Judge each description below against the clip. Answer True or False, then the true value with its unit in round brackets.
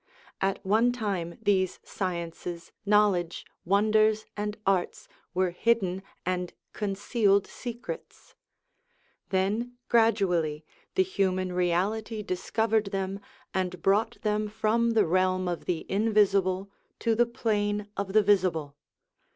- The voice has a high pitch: True (200 Hz)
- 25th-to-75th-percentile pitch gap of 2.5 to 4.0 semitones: True (2.8 semitones)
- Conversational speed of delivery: False (110 wpm)